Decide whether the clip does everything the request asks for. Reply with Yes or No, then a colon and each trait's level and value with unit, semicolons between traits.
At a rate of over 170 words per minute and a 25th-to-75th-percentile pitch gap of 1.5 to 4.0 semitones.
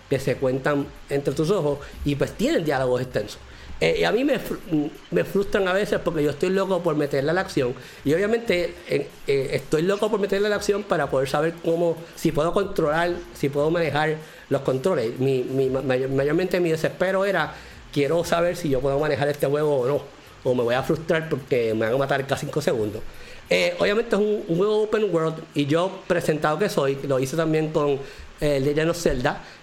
No: fast, 205 wpm; average, 4.9 semitones